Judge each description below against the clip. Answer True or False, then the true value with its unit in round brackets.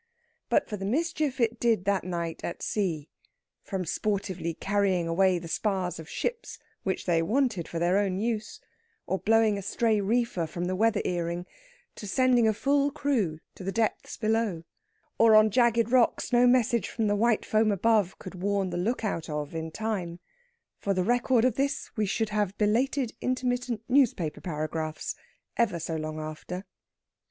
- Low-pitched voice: False (205 Hz)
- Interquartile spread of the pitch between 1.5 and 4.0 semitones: False (4.8 semitones)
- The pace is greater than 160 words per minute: True (170 wpm)